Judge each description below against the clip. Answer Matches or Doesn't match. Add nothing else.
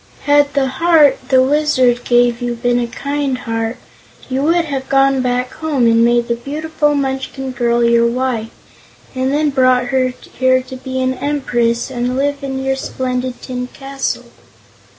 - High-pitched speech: Matches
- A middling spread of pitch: Doesn't match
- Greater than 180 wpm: Doesn't match